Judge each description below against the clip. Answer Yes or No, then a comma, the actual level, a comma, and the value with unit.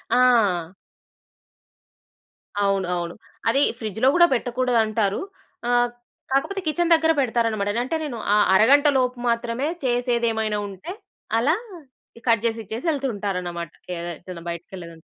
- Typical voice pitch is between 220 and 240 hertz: Yes, high, 230 Hz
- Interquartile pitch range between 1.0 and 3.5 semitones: No, average, 4.6 semitones